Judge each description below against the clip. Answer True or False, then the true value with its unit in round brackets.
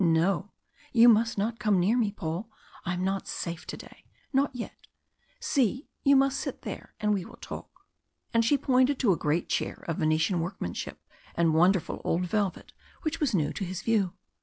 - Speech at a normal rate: True (185 wpm)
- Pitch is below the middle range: False (200 Hz)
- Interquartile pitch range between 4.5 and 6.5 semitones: True (5.4 semitones)